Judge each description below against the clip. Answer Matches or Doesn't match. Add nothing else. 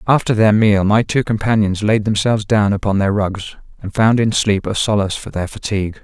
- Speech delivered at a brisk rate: Matches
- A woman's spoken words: Doesn't match